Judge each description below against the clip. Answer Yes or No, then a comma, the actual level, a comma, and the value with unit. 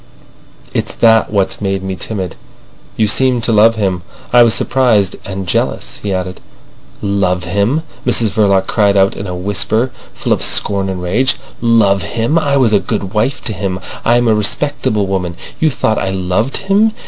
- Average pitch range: Yes, average, 3.6 semitones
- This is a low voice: Yes, low, 105 Hz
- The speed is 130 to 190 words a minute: Yes, average, 175 wpm